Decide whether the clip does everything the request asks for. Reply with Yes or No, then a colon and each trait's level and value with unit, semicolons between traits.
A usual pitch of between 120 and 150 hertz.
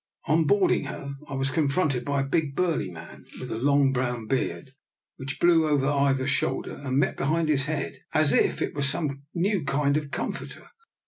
Yes: medium, 140 Hz